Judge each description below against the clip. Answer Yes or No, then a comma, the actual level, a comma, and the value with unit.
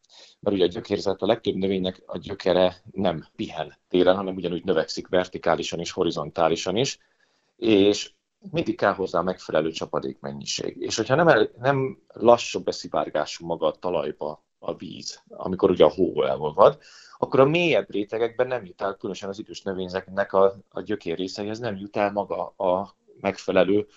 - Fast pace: Yes, fast, 160 wpm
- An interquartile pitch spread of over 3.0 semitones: Yes, average, 3.5 semitones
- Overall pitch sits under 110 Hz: Yes, low, 100 Hz